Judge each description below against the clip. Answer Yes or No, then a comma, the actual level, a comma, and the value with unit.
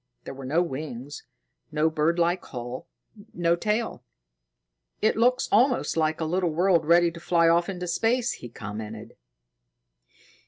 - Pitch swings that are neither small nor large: Yes, average, 3.0 semitones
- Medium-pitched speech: Yes, medium, 170 Hz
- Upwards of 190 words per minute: No, average, 140 wpm